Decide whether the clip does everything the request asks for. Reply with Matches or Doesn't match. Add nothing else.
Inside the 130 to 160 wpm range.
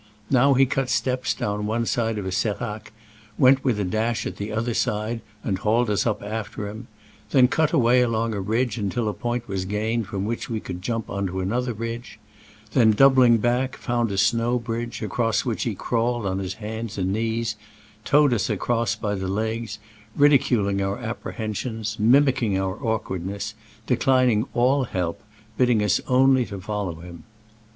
Doesn't match